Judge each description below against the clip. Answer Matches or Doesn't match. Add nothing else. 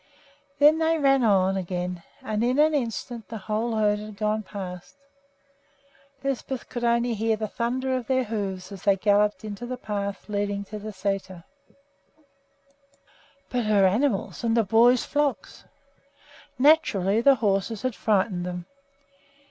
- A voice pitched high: Matches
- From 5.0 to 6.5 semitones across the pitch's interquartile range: Doesn't match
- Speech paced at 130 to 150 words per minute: Matches